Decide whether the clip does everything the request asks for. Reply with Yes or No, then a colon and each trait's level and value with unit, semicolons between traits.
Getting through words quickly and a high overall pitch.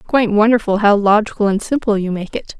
Yes: fast, 230 wpm; high, 210 Hz